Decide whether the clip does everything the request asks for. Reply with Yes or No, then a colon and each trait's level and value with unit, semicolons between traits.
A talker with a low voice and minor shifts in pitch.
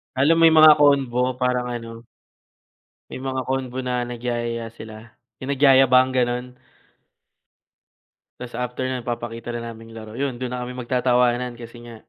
Yes: low, 125 Hz; narrow, 1.6 semitones